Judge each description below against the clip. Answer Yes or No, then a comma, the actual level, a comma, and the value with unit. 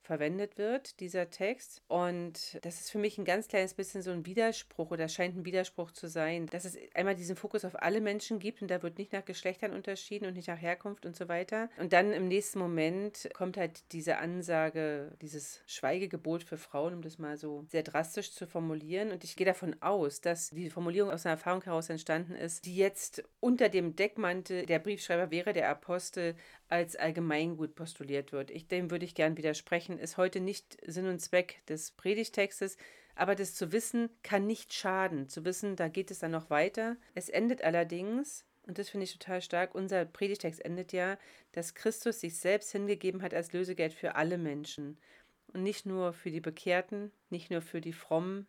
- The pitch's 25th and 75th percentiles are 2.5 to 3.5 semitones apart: Yes, average, 3.2 semitones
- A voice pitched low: No, medium, 180 Hz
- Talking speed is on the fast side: Yes, fast, 195 wpm